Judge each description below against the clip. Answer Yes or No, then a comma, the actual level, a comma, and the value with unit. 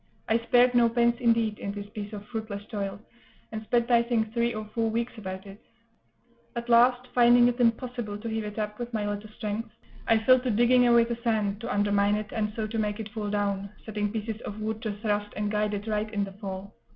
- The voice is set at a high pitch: Yes, high, 220 Hz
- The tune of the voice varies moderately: No, narrow, 2.2 semitones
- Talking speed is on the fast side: Yes, fast, 225 wpm